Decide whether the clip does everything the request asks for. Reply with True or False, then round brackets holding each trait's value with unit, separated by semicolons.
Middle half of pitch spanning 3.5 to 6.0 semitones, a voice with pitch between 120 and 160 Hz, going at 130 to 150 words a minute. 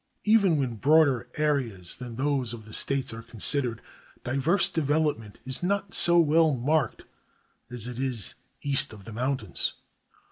True (4.8 semitones; 135 Hz; 145 wpm)